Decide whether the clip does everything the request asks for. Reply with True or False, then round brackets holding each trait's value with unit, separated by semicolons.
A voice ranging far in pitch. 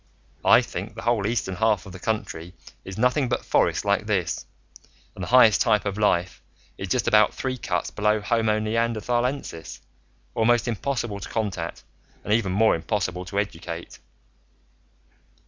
False (3.6 semitones)